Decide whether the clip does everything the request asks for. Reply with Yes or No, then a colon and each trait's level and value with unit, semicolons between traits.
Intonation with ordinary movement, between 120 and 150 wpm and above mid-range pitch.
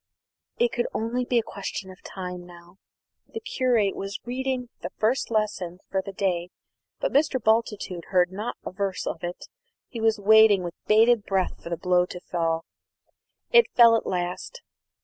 No: average, 4.7 semitones; average, 170 wpm; high, 200 Hz